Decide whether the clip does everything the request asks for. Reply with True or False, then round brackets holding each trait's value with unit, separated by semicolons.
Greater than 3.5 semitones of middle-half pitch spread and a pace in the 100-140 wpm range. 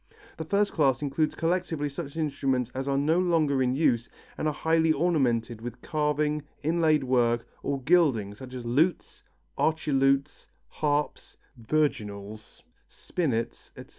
True (4.0 semitones; 135 wpm)